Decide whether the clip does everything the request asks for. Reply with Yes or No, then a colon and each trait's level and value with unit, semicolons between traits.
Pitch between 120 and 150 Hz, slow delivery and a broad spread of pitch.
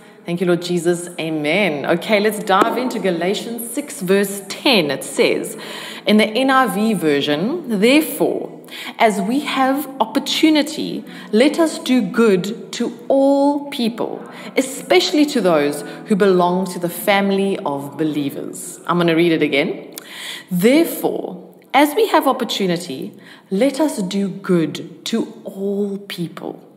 No: high, 205 Hz; slow, 130 wpm; wide, 6.4 semitones